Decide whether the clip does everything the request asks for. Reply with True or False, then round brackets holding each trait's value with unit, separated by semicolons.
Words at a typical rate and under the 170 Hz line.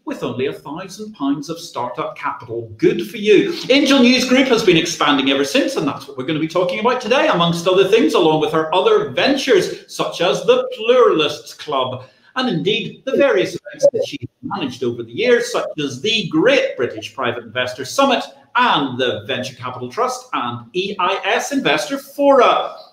False (180 wpm; 210 Hz)